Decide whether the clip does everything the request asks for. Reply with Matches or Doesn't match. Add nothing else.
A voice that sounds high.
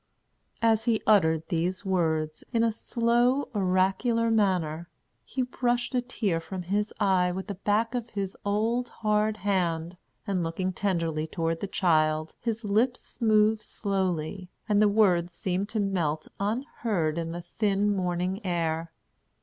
Matches